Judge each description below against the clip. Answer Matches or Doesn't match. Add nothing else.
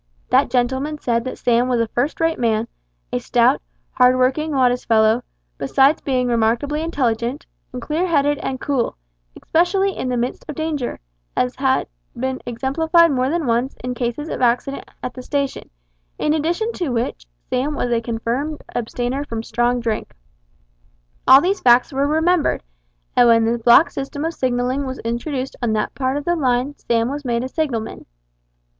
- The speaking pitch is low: Doesn't match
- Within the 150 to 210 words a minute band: Matches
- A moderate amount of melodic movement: Matches